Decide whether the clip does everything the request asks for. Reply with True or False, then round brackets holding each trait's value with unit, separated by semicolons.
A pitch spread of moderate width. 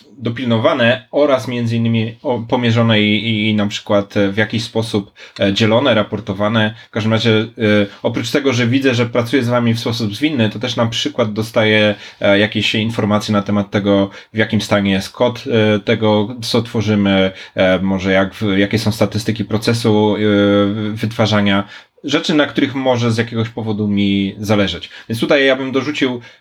False (2.3 semitones)